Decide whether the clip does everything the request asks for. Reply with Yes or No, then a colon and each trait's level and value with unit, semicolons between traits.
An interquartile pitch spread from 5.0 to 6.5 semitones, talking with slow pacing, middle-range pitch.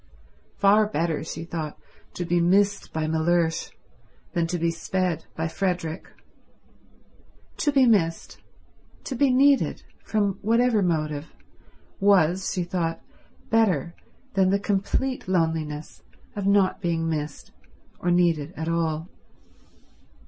No: average, 3.7 semitones; slow, 120 wpm; medium, 175 Hz